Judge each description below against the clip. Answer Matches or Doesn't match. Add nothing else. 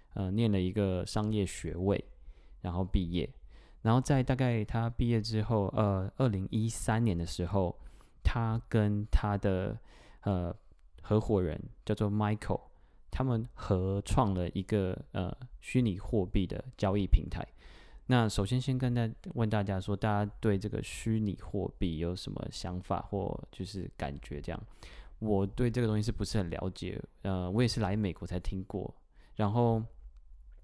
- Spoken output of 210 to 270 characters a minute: Matches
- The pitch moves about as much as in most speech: Matches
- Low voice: Matches